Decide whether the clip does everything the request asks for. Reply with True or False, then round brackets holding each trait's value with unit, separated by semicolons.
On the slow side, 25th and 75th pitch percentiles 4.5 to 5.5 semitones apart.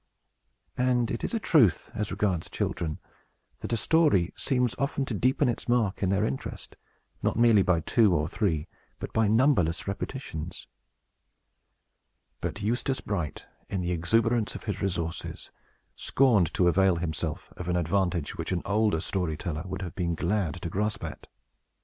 False (160 wpm; 4.9 semitones)